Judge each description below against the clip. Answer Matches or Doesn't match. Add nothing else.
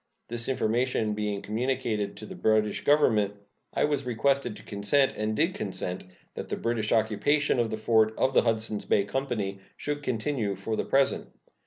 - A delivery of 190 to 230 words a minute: Doesn't match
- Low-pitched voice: Matches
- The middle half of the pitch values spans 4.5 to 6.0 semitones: Doesn't match